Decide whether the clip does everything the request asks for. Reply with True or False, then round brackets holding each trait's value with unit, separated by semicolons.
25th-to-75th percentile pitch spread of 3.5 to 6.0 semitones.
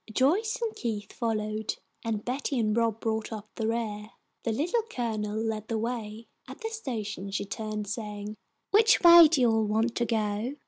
False (2.8 semitones)